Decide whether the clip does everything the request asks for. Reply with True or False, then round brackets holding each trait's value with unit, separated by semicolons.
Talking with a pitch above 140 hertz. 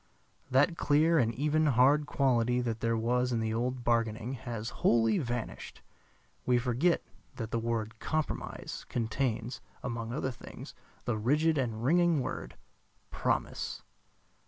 False (120 Hz)